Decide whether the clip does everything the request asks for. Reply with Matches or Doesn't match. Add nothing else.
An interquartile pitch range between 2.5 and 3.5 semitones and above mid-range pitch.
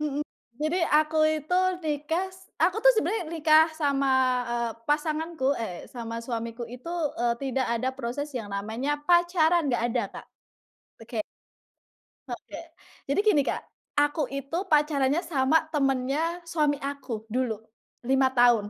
Doesn't match